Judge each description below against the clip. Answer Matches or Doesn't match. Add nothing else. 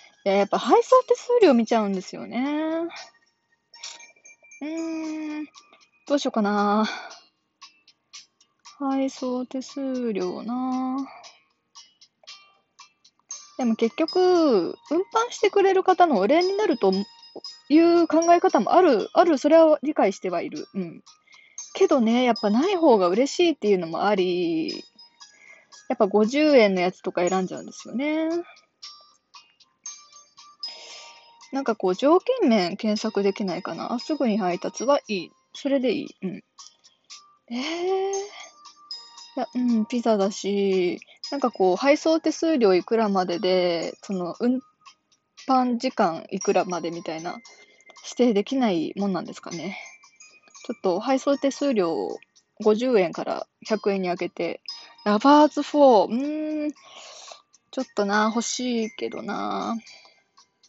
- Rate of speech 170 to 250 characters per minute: Matches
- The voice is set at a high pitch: Matches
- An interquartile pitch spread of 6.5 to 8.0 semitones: Matches